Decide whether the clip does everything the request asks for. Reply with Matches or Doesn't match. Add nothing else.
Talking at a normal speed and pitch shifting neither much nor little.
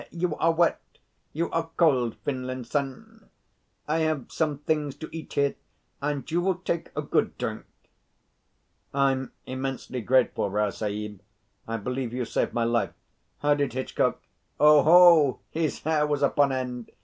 Matches